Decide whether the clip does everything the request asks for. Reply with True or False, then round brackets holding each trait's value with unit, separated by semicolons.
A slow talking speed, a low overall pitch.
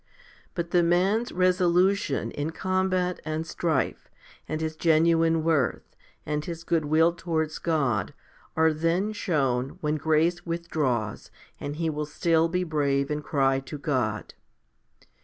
False (130 wpm; 160 Hz)